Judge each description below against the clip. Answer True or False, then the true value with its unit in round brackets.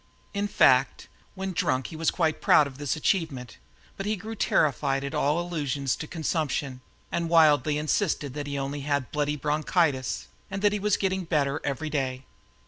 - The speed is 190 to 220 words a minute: False (170 wpm)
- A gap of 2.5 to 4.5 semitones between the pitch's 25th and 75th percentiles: True (3.6 semitones)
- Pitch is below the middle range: False (150 Hz)